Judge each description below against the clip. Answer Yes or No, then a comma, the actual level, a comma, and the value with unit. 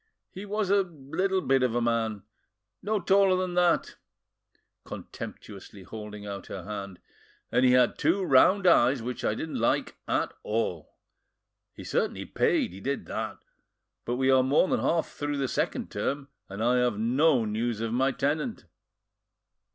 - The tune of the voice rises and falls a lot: Yes, wide, 6.9 semitones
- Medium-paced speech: Yes, average, 155 wpm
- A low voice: Yes, low, 130 Hz